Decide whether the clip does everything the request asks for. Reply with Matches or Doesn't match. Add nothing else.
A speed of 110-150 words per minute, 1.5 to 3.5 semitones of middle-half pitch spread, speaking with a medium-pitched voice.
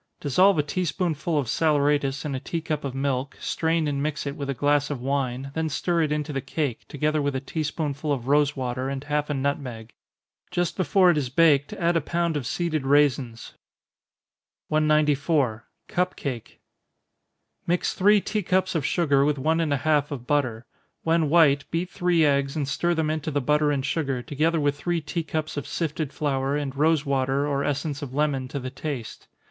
Doesn't match